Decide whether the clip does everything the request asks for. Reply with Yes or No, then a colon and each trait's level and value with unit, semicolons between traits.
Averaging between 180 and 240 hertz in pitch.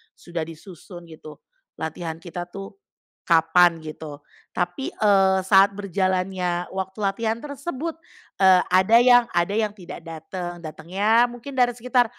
Yes: high, 190 Hz